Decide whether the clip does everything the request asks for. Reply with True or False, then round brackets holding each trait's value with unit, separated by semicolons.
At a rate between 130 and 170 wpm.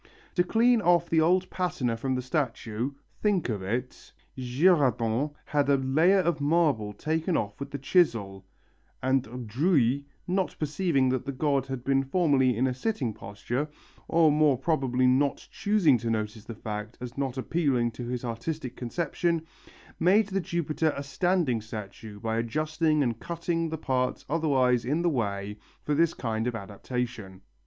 True (160 wpm)